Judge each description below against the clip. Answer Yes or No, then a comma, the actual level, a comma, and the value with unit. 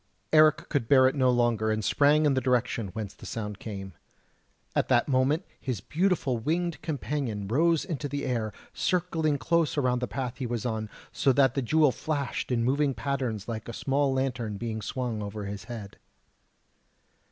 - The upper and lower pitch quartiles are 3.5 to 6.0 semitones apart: Yes, average, 4.3 semitones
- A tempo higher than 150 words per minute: Yes, average, 175 wpm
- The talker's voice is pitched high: No, low, 130 Hz